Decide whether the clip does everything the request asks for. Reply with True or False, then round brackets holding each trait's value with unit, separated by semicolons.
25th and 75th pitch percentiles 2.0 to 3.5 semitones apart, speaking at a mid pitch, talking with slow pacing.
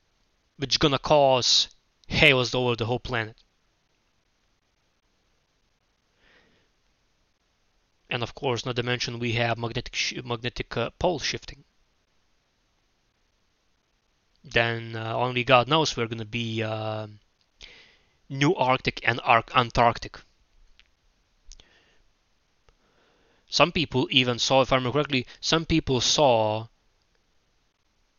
False (2.8 semitones; 120 Hz; 105 wpm)